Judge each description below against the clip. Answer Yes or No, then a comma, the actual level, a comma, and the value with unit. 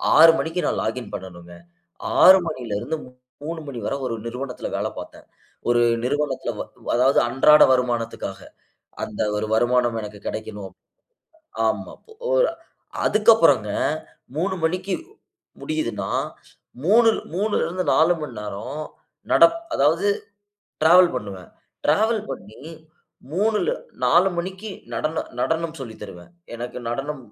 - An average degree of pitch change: No, wide, 6.9 semitones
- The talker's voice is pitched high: No, medium, 140 Hz